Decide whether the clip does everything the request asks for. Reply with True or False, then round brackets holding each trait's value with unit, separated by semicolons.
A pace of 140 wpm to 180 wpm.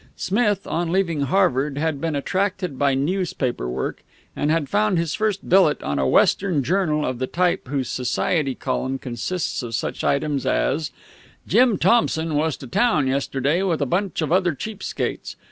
True (170 wpm)